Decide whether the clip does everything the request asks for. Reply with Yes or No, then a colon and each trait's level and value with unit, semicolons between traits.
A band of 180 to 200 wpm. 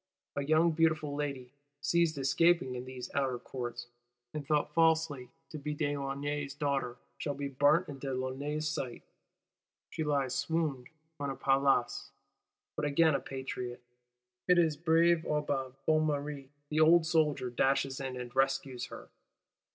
No: average, 145 wpm